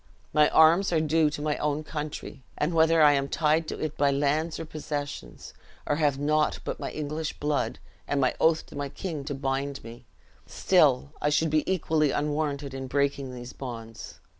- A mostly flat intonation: Yes, narrow, 1.9 semitones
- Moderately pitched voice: Yes, medium, 150 Hz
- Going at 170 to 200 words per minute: Yes, average, 190 wpm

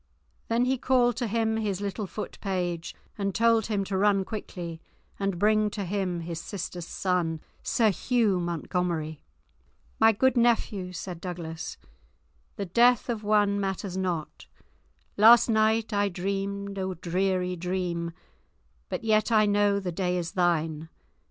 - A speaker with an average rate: Yes, average, 145 wpm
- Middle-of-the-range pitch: No, high, 195 Hz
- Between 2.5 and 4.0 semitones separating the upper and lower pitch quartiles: Yes, average, 3.3 semitones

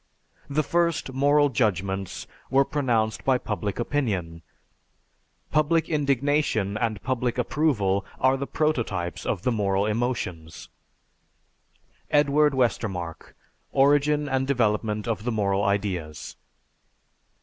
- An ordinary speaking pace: No, slow, 105 wpm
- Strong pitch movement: Yes, wide, 6.0 semitones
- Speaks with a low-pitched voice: Yes, low, 120 Hz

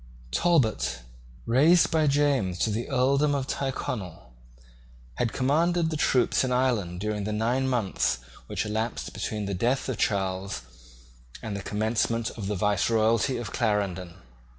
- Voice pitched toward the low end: Yes, low, 115 Hz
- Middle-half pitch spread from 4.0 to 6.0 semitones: Yes, average, 4.7 semitones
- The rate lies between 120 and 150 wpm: Yes, average, 140 wpm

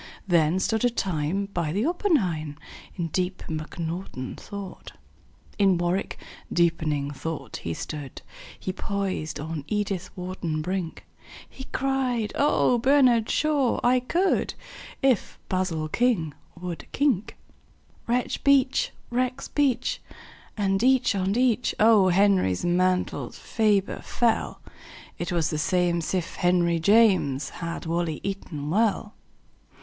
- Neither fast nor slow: No, slow, 105 wpm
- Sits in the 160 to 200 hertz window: Yes, high, 190 Hz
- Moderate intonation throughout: No, wide, 5.8 semitones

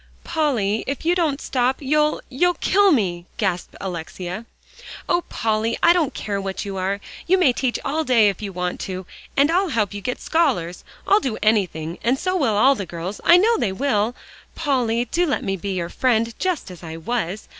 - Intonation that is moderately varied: No, wide, 7.5 semitones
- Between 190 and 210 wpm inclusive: Yes, average, 200 wpm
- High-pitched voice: Yes, high, 230 Hz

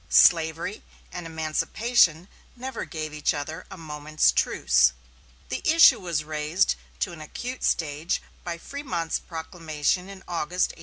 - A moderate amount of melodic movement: Yes, average, 3.1 semitones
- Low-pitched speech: No, medium, 165 Hz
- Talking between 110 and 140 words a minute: Yes, slow, 135 wpm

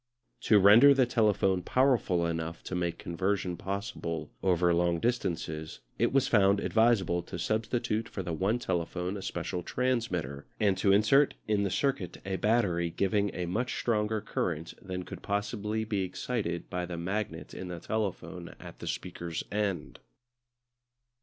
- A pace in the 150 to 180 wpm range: Yes, average, 155 wpm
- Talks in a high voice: No, very low, 95 Hz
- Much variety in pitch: No, average, 3.8 semitones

